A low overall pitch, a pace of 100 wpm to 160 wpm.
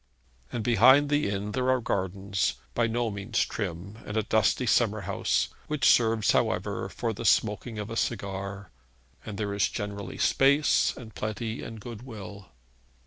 Yes: low, 110 Hz; average, 155 wpm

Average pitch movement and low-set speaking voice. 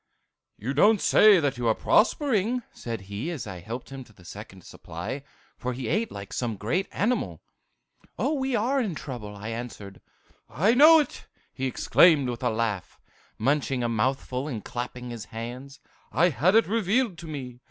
No: wide, 9.0 semitones; low, 130 Hz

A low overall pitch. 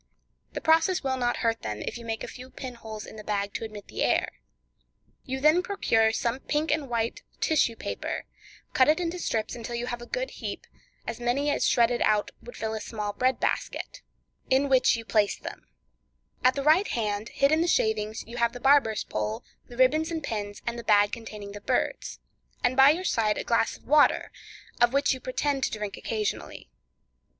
No: high, 240 Hz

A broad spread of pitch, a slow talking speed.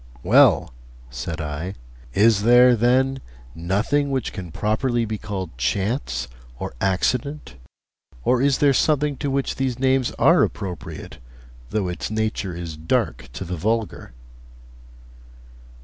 Yes: wide, 6.7 semitones; slow, 125 wpm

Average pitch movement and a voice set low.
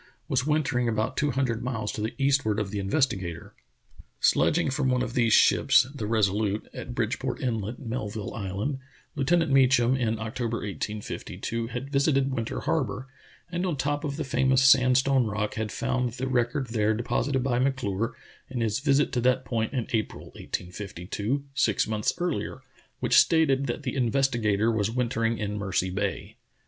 Yes: average, 3.8 semitones; low, 120 Hz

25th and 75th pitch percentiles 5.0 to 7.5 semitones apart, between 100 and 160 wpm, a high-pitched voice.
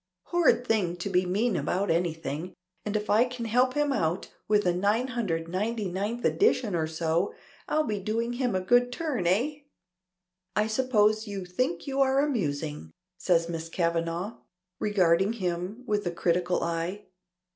Yes: wide, 5.5 semitones; average, 150 wpm; high, 200 Hz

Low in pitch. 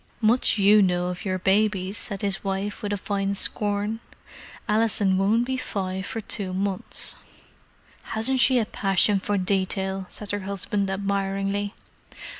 No: high, 200 Hz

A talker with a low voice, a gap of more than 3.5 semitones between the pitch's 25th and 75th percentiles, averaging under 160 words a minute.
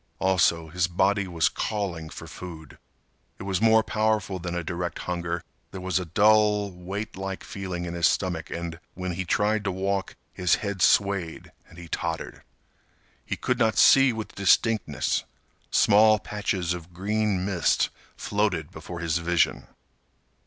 No: very low, 95 Hz; average, 3.1 semitones; average, 150 wpm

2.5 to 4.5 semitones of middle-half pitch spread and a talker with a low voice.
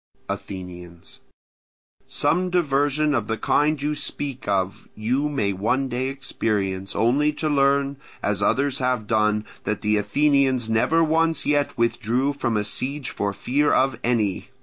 No: average, 5.1 semitones; low, 130 Hz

